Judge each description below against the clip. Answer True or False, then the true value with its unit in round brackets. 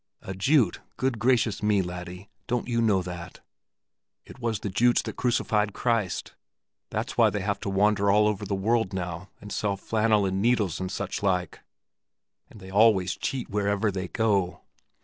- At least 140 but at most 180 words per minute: True (170 wpm)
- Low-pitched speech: True (100 Hz)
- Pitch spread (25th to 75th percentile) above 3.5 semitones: False (2.9 semitones)